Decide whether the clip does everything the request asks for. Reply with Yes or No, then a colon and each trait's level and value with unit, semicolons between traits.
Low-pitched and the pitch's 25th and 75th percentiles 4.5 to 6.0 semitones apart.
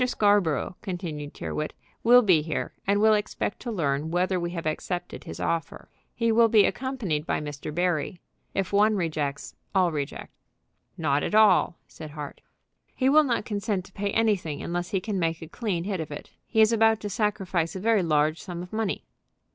No: medium, 185 Hz; average, 5.0 semitones